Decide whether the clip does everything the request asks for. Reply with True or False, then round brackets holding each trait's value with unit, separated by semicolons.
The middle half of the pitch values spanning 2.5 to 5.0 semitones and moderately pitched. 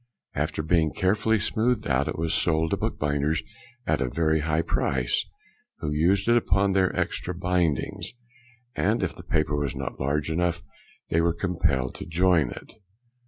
False (3.5 semitones; 80 Hz)